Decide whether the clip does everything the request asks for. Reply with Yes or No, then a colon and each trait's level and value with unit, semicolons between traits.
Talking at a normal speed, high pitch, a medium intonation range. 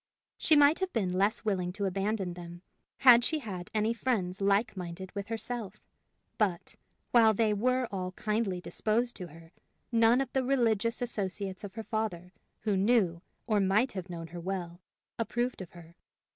Yes: average, 170 wpm; high, 205 Hz; average, 4.1 semitones